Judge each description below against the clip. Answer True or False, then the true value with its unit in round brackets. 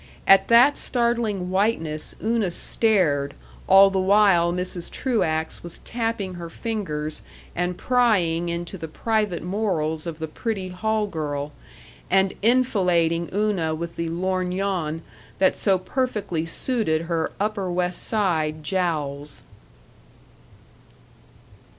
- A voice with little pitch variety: False (4.3 semitones)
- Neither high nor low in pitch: True (180 Hz)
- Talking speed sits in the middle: False (115 wpm)